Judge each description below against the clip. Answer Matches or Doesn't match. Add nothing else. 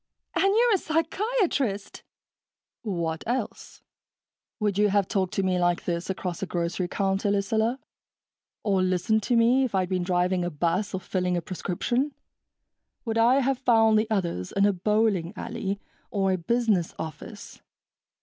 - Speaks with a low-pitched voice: Doesn't match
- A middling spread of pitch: Matches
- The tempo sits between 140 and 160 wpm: Matches